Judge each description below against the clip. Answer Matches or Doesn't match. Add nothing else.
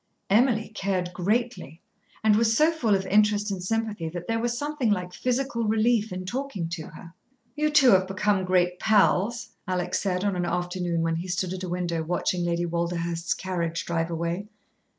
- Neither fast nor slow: Matches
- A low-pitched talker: Doesn't match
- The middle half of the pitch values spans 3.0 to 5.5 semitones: Matches